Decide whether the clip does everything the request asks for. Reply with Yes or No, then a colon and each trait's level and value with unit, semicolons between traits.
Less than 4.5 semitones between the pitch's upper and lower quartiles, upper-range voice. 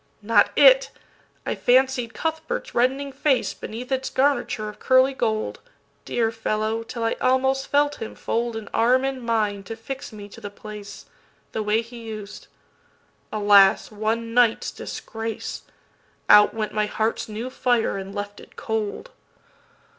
Yes: average, 3.3 semitones; high, 230 Hz